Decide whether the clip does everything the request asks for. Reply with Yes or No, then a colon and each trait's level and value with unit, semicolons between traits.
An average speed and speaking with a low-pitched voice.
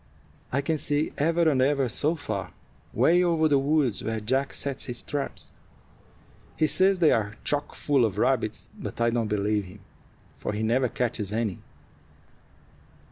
Yes: average, 165 wpm; low, 130 Hz